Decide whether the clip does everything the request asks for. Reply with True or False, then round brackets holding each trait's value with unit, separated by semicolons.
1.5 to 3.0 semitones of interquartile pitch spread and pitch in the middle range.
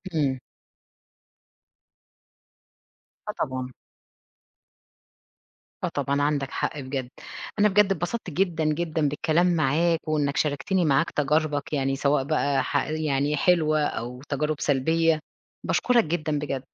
True (2.7 semitones; 150 Hz)